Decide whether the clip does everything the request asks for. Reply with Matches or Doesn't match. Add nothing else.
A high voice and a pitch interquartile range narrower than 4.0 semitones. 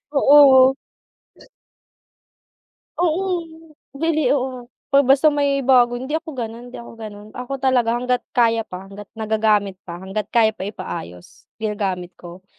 Doesn't match